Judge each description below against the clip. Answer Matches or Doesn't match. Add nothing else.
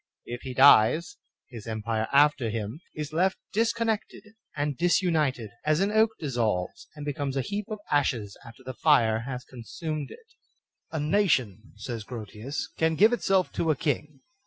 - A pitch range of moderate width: Doesn't match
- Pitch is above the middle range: Doesn't match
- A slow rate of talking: Doesn't match